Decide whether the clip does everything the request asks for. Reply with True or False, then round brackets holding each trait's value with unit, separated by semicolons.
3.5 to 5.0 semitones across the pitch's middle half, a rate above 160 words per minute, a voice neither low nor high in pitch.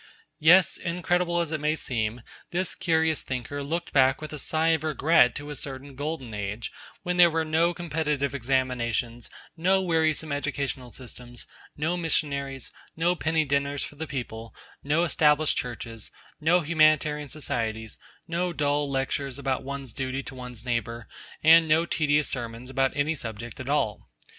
False (3.9 semitones; 155 wpm; 145 Hz)